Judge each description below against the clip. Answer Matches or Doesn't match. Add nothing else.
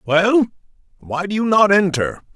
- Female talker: Doesn't match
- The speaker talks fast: Doesn't match